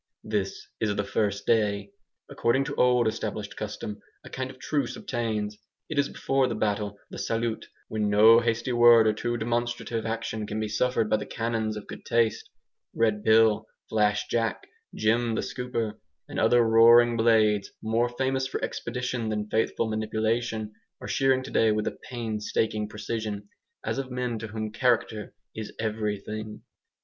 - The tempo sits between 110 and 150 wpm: No, average, 160 wpm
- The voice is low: Yes, low, 110 Hz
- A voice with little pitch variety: Yes, narrow, 1.9 semitones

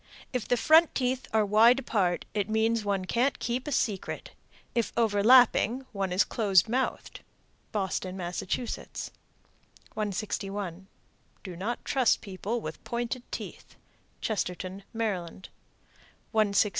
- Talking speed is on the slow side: Yes, slow, 120 wpm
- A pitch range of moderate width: Yes, average, 3.6 semitones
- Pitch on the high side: Yes, high, 215 Hz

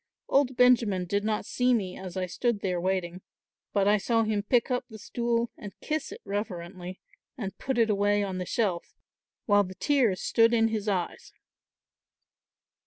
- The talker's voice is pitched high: Yes, high, 205 Hz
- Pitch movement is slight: No, average, 3.8 semitones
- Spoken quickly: No, average, 175 wpm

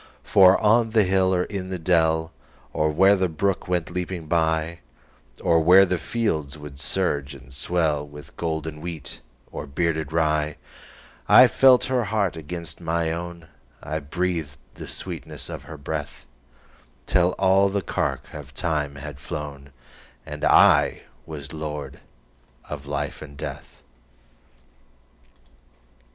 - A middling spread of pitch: Yes, average, 3.8 semitones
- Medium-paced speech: No, slow, 120 wpm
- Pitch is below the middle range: Yes, very low, 80 Hz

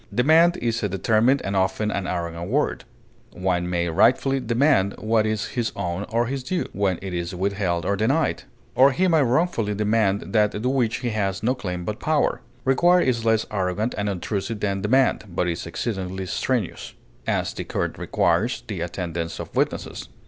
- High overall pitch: No, low, 105 Hz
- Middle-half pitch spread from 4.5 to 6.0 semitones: Yes, average, 4.8 semitones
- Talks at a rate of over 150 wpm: Yes, average, 180 wpm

